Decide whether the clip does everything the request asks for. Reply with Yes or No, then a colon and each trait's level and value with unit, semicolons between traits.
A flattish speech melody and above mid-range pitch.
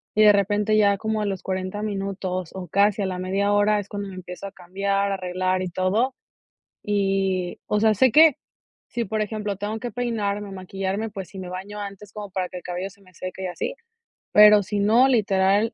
Yes: narrow, 2.0 semitones; high, 200 Hz